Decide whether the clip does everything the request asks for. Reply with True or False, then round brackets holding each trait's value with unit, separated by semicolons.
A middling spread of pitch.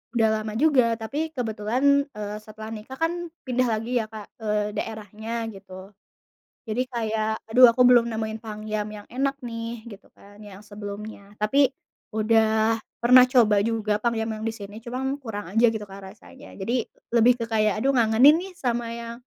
False (2.1 semitones)